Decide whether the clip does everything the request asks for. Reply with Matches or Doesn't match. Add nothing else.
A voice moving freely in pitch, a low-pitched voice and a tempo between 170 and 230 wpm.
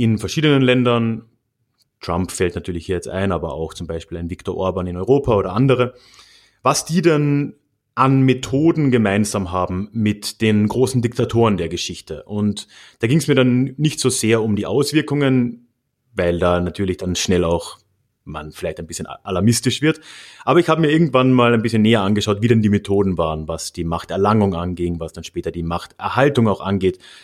Matches